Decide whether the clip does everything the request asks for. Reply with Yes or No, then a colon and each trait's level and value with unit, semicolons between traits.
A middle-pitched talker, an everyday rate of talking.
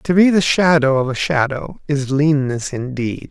Yes: medium, 145 Hz; average, 180 wpm